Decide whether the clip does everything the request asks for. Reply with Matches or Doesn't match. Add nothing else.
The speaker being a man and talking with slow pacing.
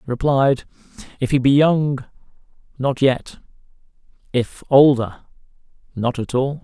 Matches